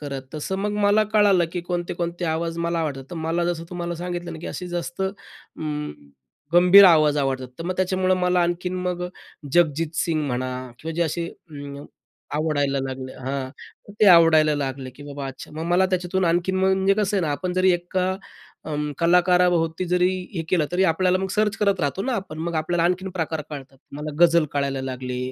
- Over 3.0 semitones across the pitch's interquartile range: Yes, average, 3.4 semitones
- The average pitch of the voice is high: No, medium, 170 Hz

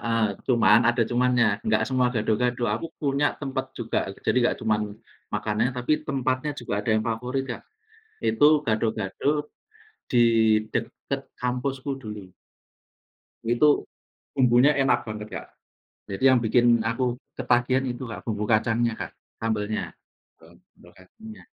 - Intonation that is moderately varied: Yes, average, 3.1 semitones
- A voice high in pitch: No, low, 120 Hz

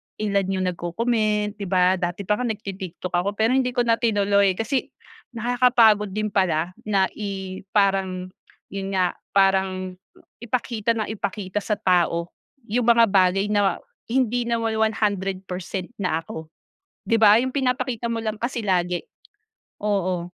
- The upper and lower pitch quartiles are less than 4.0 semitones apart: Yes, average, 3.4 semitones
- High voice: Yes, high, 205 Hz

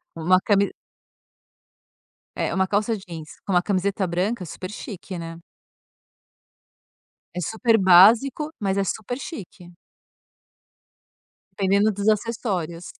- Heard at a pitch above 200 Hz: No, high, 195 Hz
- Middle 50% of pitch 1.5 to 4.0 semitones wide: Yes, average, 3.3 semitones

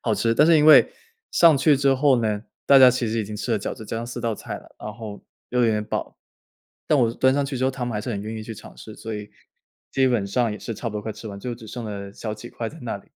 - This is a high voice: No, low, 115 Hz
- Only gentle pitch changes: No, average, 3.3 semitones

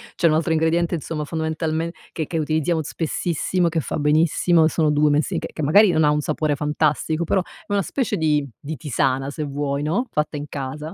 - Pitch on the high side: No, medium, 155 Hz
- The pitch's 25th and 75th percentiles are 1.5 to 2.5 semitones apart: Yes, narrow, 1.8 semitones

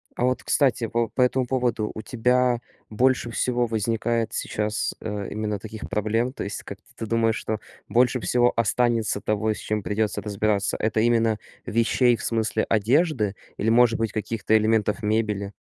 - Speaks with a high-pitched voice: No, low, 115 Hz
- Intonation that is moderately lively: No, narrow, 2.1 semitones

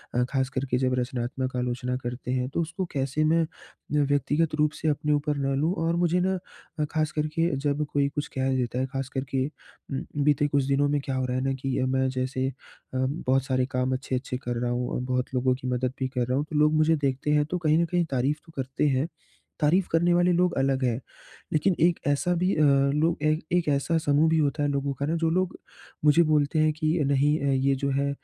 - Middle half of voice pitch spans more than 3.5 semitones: No, average, 3.0 semitones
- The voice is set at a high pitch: No, medium, 140 Hz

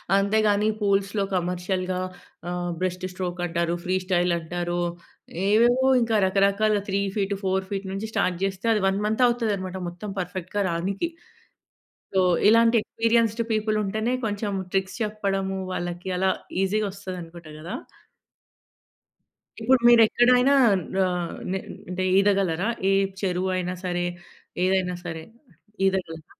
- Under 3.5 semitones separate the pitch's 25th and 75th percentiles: Yes, average, 2.8 semitones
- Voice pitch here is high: Yes, high, 195 Hz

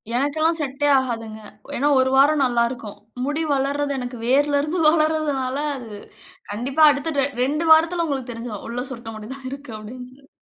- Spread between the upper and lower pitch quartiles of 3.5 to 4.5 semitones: No, average, 3.1 semitones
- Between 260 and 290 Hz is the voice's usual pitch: Yes, very high, 275 Hz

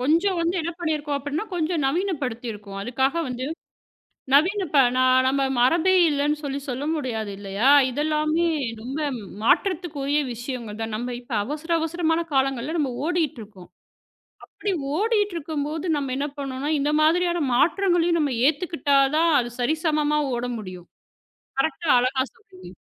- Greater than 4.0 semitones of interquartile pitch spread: Yes, average, 4.5 semitones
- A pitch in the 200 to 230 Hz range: No, very high, 290 Hz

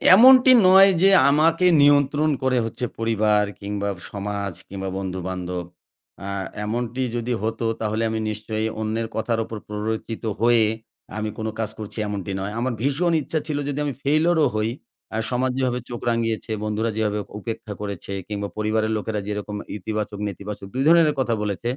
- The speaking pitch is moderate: No, low, 110 Hz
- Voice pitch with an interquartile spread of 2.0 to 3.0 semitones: No, average, 3.6 semitones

